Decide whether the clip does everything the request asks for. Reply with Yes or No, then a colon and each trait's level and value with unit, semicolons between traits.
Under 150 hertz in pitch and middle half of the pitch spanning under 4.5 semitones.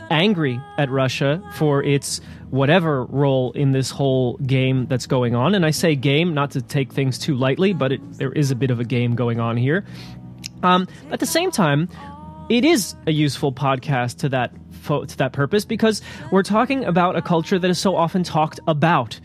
No: medium, 140 Hz; average, 4.8 semitones